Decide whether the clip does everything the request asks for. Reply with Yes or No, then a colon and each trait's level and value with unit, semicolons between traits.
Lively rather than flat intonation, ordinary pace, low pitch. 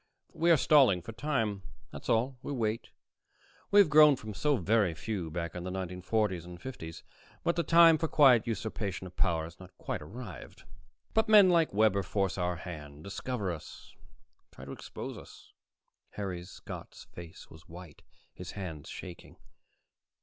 Yes: wide, 6.5 semitones; average, 165 wpm; low, 100 Hz